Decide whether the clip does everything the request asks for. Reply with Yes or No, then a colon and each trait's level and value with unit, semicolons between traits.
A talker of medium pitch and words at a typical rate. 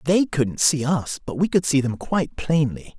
No: medium, 150 Hz; fast, 220 wpm